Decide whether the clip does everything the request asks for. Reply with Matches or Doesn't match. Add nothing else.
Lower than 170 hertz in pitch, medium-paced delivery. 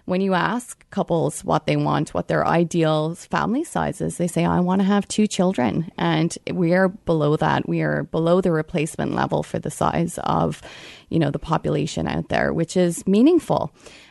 Doesn't match